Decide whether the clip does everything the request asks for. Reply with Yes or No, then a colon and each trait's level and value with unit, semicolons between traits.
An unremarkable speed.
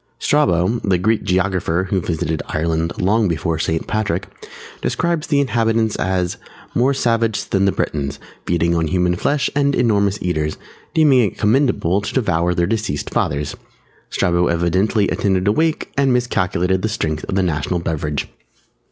Yes: average, 150 wpm